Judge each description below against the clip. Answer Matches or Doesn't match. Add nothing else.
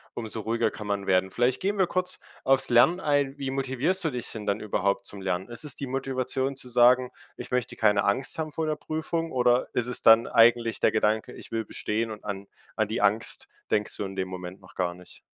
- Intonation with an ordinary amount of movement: Matches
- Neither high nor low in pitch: Doesn't match